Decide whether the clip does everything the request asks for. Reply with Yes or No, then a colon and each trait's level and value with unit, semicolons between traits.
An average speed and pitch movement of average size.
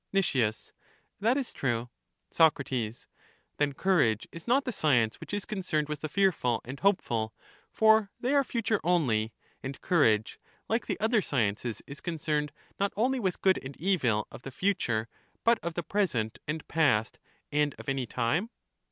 No: average, 165 wpm; wide, 8.2 semitones